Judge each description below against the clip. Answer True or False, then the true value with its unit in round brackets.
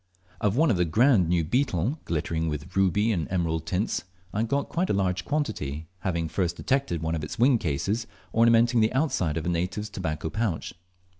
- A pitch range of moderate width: False (6.0 semitones)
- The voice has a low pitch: True (95 Hz)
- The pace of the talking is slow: False (170 wpm)